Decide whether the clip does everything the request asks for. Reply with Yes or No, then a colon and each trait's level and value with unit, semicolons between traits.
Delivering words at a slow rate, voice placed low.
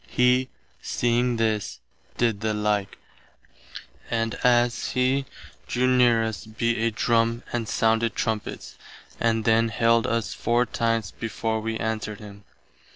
Yes: slow, 130 wpm; low, 115 Hz